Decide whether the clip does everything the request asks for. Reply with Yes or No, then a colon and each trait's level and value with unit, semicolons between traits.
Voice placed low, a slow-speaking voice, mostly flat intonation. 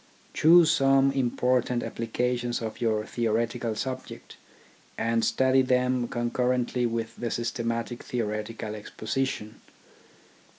Yes: low, 120 Hz; slow, 100 wpm; narrow, 1.9 semitones